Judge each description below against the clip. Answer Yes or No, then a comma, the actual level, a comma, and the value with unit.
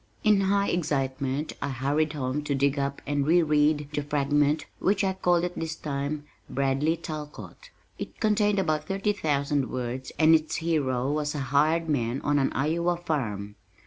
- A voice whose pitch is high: No, medium, 150 Hz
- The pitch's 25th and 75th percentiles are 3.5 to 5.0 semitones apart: No, average, 3.1 semitones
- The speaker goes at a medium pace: Yes, average, 170 wpm